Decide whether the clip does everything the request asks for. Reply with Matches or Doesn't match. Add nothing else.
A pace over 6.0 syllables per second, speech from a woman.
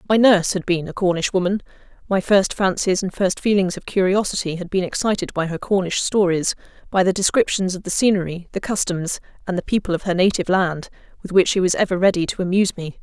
Matches